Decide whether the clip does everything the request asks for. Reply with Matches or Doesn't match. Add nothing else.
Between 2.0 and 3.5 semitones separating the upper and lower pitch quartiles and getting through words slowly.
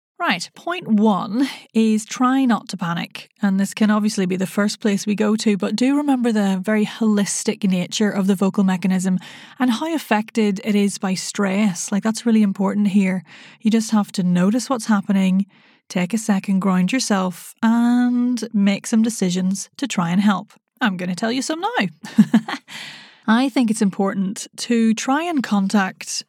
Doesn't match